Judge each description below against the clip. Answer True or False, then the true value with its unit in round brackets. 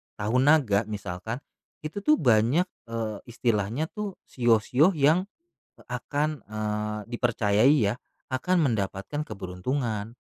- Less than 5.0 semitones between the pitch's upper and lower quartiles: False (5.5 semitones)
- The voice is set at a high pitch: False (115 Hz)